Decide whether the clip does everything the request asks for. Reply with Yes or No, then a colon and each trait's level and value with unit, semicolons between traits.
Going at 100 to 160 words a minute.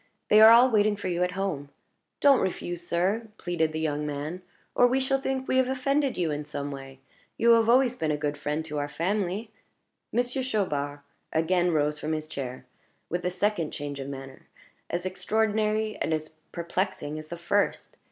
No: average, 190 wpm